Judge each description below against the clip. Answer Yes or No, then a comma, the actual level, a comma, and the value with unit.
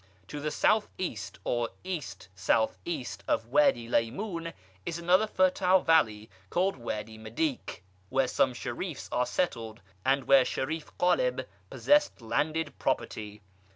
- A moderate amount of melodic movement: No, wide, 7.8 semitones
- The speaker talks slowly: Yes, slow, 130 wpm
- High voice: No, medium, 140 Hz